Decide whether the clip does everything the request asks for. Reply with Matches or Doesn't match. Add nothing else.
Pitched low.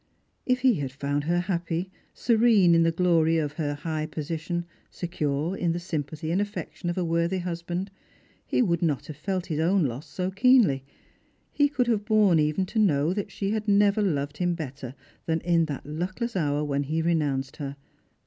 Doesn't match